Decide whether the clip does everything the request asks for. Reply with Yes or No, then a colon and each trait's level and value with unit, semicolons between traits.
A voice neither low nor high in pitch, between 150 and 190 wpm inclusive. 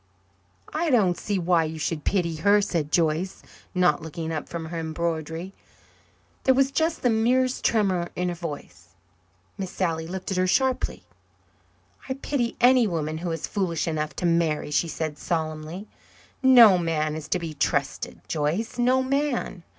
Yes: medium, 175 Hz; average, 160 wpm